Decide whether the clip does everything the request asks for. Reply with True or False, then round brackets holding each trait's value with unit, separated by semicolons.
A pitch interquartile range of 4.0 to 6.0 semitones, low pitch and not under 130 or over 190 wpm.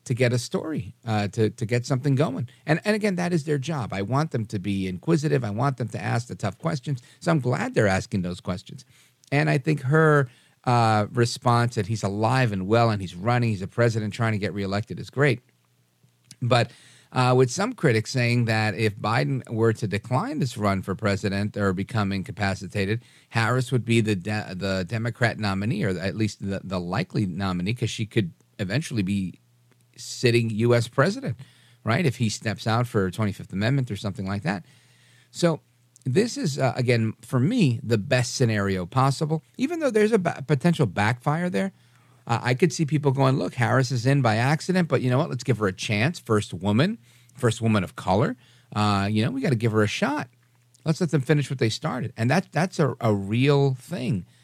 False (4.5 semitones; 120 Hz; 205 wpm)